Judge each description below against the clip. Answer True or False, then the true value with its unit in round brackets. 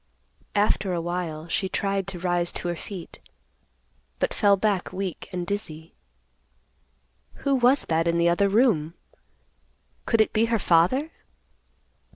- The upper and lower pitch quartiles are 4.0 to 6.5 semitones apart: False (3.6 semitones)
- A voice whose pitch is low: False (185 Hz)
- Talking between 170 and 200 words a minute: False (135 wpm)